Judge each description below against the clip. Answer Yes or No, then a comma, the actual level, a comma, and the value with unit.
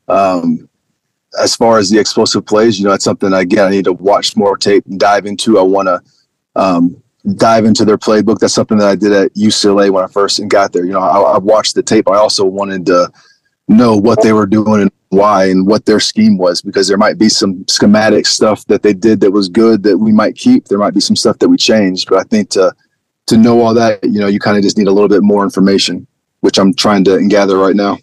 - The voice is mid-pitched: No, low, 105 Hz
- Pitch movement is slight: Yes, narrow, 2.2 semitones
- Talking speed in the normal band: No, fast, 250 wpm